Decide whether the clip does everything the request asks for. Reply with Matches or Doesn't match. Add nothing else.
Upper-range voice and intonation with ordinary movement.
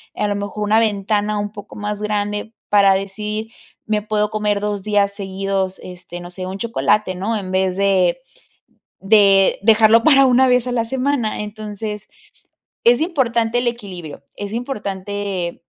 Doesn't match